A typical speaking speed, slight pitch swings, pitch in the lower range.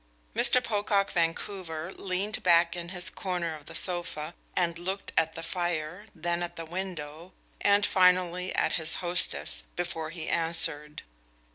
No: average, 145 wpm; narrow, 2.2 semitones; medium, 175 Hz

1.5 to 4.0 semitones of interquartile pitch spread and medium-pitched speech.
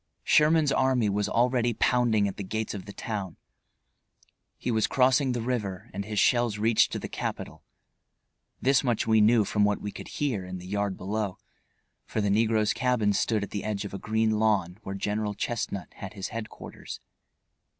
No: average, 2.8 semitones; low, 110 Hz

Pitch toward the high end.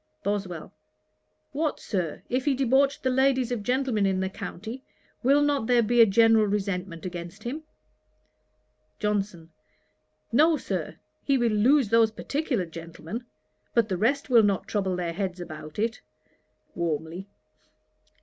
Yes: high, 215 Hz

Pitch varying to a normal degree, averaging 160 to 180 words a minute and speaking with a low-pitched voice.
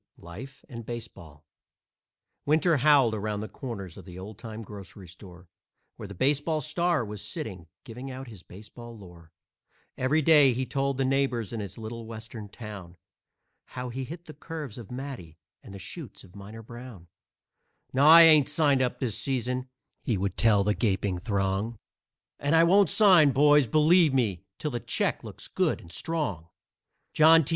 No: wide, 5.9 semitones; average, 170 wpm; low, 120 Hz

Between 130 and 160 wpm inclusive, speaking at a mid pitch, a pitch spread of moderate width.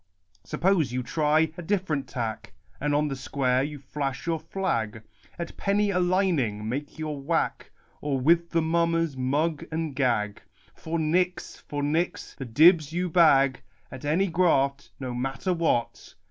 Yes: average, 155 wpm; medium, 150 Hz; average, 4.0 semitones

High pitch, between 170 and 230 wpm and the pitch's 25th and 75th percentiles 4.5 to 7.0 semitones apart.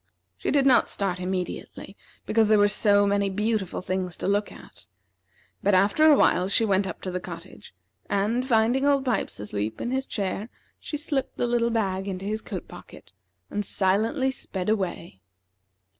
No: high, 205 Hz; average, 175 wpm; average, 3.8 semitones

